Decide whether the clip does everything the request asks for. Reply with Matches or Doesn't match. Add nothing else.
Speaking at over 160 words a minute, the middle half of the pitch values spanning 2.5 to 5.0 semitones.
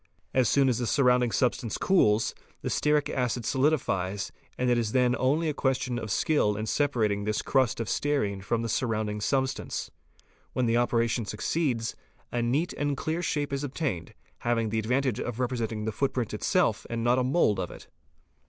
Matches